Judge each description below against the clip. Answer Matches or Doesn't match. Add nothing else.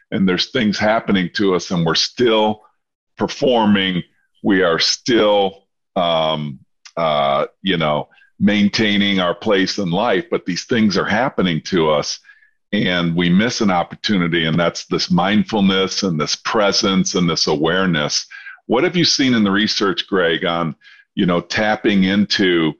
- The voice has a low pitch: Matches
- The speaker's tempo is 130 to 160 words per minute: Matches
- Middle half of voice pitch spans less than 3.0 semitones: Doesn't match